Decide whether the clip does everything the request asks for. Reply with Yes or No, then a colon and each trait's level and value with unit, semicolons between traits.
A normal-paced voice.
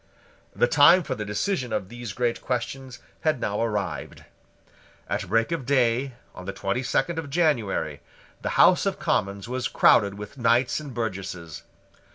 Yes: average, 160 wpm